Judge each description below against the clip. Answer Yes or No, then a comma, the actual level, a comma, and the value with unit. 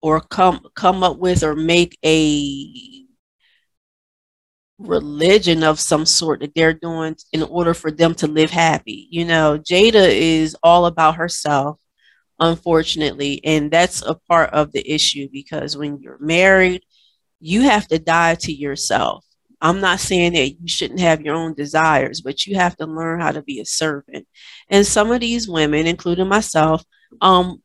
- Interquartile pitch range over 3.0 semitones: No, narrow, 2.6 semitones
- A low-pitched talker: No, medium, 165 Hz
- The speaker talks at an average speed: Yes, average, 165 wpm